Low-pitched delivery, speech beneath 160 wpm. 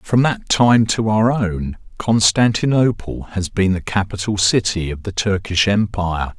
Yes: low, 105 Hz; average, 150 wpm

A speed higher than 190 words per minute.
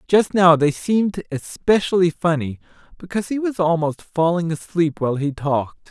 No: average, 150 wpm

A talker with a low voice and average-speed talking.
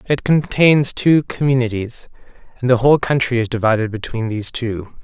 Yes: low, 125 Hz; average, 155 wpm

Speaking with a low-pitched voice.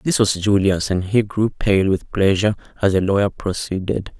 Yes: low, 100 Hz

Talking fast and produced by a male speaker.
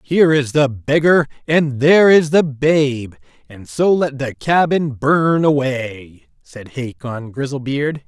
No: average, 140 wpm; male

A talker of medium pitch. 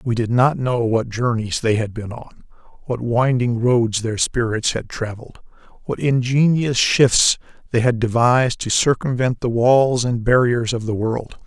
No: low, 120 Hz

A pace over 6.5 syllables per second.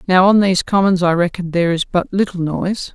No: 6.1 syllables/s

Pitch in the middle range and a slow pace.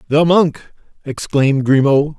Yes: medium, 145 Hz; slow, 110 wpm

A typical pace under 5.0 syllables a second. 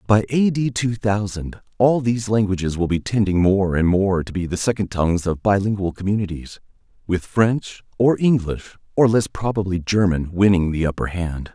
No: 5.1 syllables/s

